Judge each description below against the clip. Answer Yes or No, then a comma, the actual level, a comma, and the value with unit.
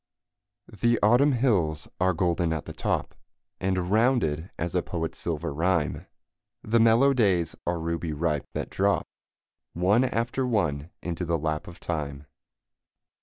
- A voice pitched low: Yes, very low, 90 Hz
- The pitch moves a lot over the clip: Yes, wide, 5.7 semitones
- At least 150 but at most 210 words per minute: No, average, 140 wpm